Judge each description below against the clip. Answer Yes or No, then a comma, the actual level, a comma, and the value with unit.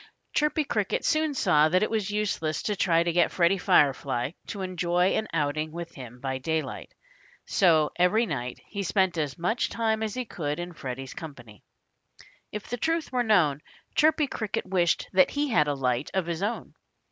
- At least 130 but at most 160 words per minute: No, average, 180 wpm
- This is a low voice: No, medium, 175 Hz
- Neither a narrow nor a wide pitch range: No, wide, 6.1 semitones